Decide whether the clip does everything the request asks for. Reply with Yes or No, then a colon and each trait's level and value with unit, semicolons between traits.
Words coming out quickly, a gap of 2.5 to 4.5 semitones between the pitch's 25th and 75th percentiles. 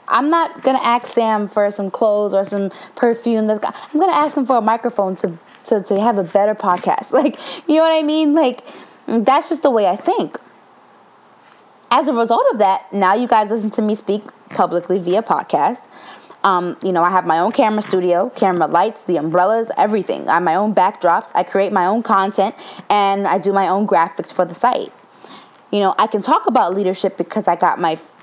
Yes: fast, 210 wpm; average, 4.0 semitones